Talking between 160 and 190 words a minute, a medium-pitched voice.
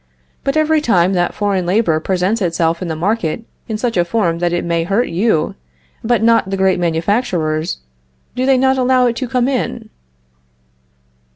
No: average, 175 wpm; high, 195 Hz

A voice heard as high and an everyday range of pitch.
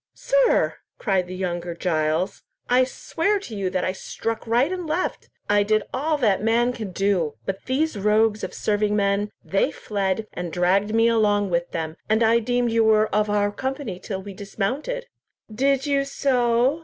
Yes: high, 215 Hz; average, 4.3 semitones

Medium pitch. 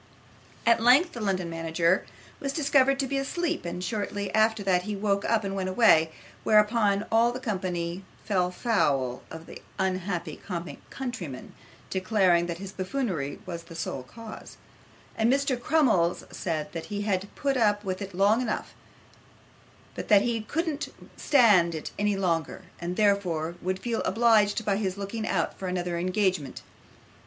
No: high, 200 Hz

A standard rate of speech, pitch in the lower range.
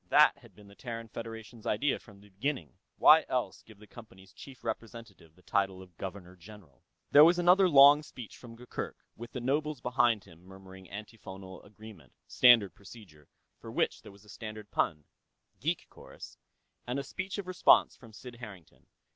Yes: average, 175 wpm; low, 110 Hz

